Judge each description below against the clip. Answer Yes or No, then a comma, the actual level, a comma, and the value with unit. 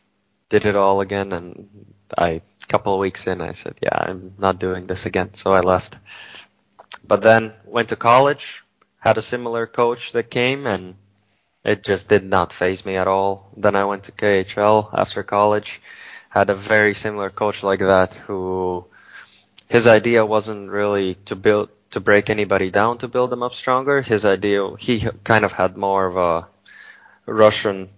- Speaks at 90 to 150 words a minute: No, average, 175 wpm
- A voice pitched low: Yes, low, 100 Hz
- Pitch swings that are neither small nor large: No, narrow, 2.1 semitones